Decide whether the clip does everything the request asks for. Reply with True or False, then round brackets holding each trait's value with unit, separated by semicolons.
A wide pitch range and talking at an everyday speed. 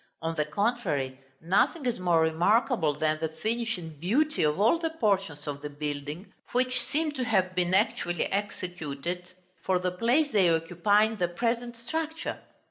True (6.6 semitones; 165 wpm)